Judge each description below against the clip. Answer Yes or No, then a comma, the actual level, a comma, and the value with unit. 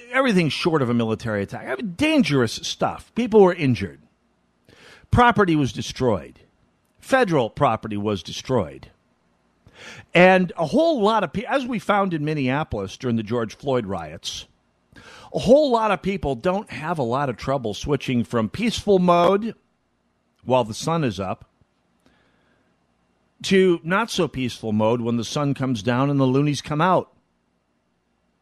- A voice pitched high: No, low, 135 Hz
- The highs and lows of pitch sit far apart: Yes, wide, 8.7 semitones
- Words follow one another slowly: No, average, 150 wpm